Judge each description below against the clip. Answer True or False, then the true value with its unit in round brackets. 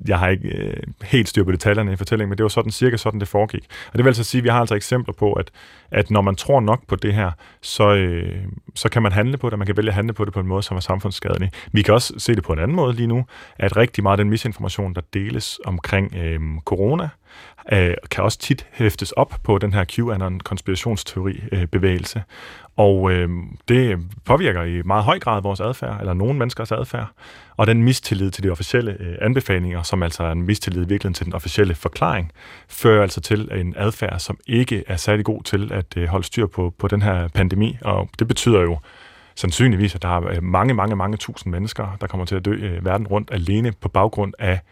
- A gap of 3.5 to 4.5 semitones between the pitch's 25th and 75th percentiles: False (2.9 semitones)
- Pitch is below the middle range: True (100 Hz)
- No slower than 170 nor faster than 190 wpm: False (215 wpm)